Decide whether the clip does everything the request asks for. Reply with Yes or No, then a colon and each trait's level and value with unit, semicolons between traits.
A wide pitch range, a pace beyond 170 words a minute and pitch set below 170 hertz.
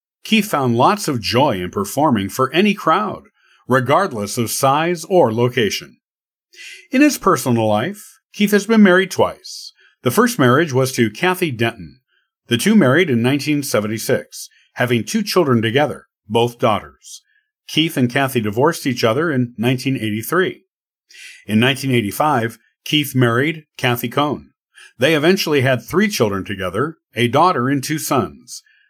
No: wide, 7.3 semitones; average, 140 wpm; low, 135 Hz